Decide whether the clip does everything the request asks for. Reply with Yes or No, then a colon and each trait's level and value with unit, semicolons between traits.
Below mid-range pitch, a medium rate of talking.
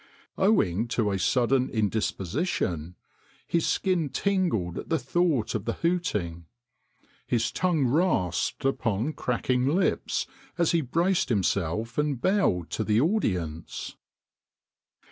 No: low, 125 Hz; slow, 115 wpm